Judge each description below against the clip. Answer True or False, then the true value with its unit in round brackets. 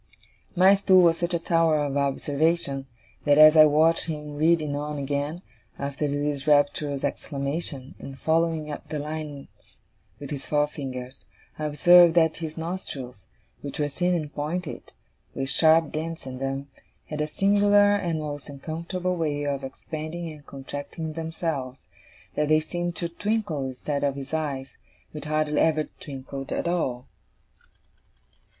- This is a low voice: False (150 Hz)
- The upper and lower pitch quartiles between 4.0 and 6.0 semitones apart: False (2.6 semitones)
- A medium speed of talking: True (145 wpm)